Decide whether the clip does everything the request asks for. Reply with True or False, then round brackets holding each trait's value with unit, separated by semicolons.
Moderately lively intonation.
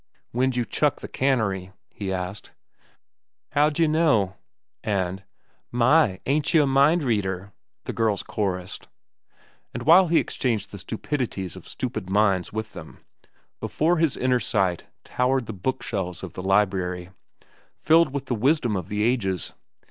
False (6.1 semitones)